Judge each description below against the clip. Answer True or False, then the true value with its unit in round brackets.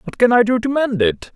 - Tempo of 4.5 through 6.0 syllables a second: True (5.7 syllables/s)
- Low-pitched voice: False (220 Hz)